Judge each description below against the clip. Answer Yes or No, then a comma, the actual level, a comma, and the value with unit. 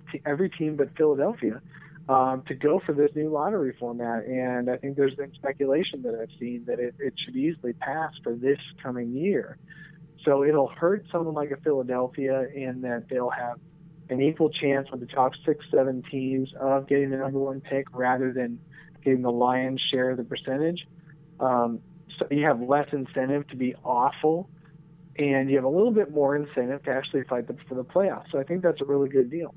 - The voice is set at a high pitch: No, medium, 140 Hz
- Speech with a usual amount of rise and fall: Yes, average, 3.3 semitones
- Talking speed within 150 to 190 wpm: No, average, 200 wpm